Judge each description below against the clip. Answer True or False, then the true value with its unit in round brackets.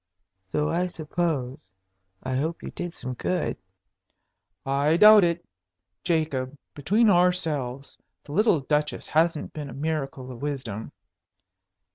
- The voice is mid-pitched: True (150 Hz)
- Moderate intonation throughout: True (4.1 semitones)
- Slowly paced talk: True (120 wpm)